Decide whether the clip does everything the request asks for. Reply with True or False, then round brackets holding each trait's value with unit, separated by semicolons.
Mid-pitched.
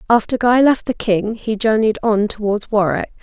False (220 Hz)